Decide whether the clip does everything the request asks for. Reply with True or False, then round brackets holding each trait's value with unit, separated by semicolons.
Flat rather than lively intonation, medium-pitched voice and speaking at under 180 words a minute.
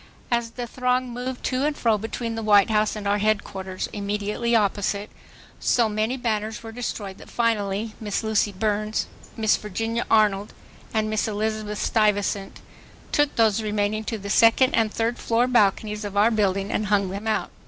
False (1.9 semitones; 215 Hz; 170 wpm)